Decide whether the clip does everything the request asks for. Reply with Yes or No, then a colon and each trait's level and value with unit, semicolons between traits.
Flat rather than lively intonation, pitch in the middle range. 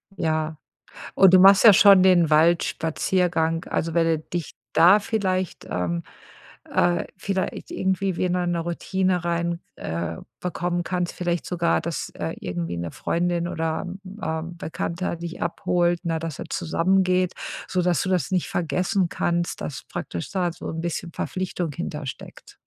Yes: narrow, 2.0 semitones; medium, 175 Hz